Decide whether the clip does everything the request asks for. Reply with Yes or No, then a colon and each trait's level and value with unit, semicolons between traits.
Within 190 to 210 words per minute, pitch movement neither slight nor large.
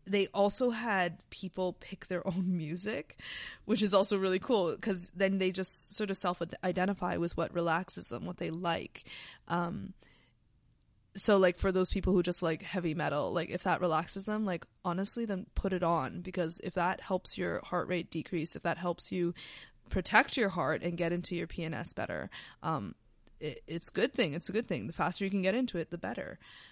No: average, 200 wpm; narrow, 2.2 semitones